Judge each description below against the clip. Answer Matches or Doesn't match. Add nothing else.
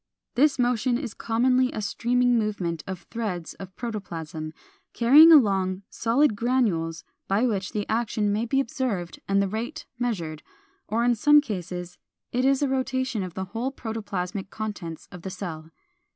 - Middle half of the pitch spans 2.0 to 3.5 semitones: Doesn't match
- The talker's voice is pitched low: Doesn't match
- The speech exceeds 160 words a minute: Doesn't match